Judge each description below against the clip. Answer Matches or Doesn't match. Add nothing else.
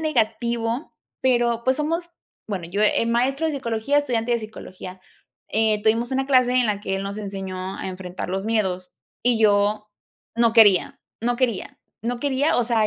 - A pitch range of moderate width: Matches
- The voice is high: Matches